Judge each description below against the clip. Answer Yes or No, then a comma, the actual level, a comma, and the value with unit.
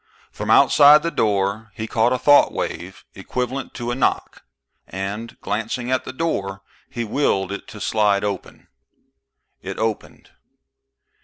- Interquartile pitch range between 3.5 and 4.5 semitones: Yes, average, 4.1 semitones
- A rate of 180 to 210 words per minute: No, average, 140 wpm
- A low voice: Yes, low, 110 Hz